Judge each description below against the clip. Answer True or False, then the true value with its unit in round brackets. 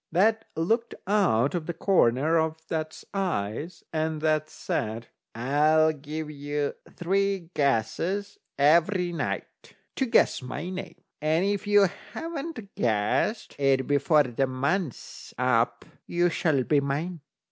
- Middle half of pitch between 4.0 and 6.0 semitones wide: True (5.0 semitones)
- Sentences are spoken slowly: True (125 wpm)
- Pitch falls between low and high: True (160 Hz)